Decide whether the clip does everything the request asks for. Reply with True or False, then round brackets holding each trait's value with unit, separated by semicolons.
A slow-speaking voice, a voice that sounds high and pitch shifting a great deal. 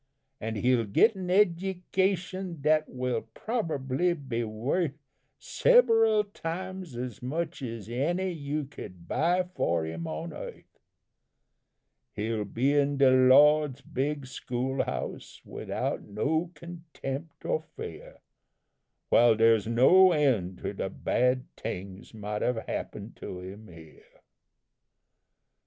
False (115 wpm; 135 Hz; 7.2 semitones)